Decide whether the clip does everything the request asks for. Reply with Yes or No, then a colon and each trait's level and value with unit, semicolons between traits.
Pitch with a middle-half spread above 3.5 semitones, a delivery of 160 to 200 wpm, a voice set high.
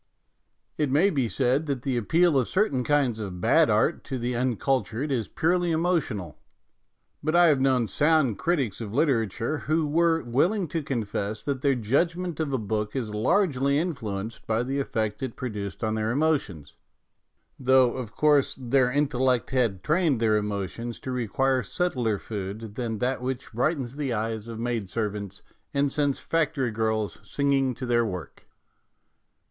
No: average, 4.7 semitones; average, 165 wpm; low, 130 Hz